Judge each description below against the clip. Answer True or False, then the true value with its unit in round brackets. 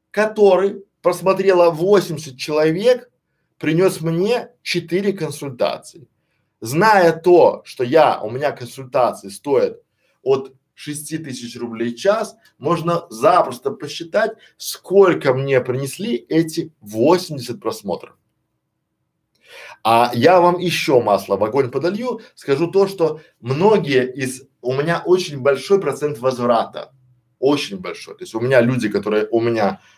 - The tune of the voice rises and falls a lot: True (6.8 semitones)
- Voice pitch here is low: False (160 Hz)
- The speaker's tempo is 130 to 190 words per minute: False (120 wpm)